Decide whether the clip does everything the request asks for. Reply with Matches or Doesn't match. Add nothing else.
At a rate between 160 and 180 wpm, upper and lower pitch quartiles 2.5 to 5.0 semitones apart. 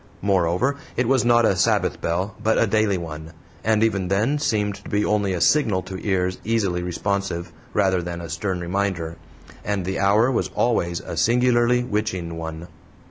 Matches